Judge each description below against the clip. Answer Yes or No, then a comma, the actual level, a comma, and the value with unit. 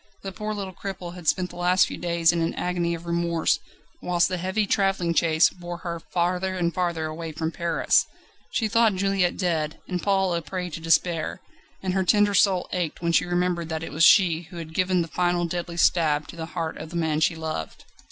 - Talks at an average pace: No, fast, 215 wpm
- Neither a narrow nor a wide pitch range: No, narrow, 1.9 semitones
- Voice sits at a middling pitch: Yes, medium, 175 Hz